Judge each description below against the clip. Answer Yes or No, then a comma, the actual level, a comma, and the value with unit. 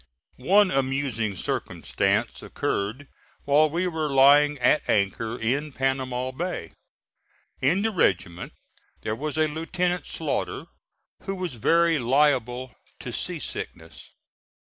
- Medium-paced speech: No, slow, 115 wpm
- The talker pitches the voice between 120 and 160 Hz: Yes, medium, 140 Hz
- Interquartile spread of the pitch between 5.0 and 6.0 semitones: No, average, 4.6 semitones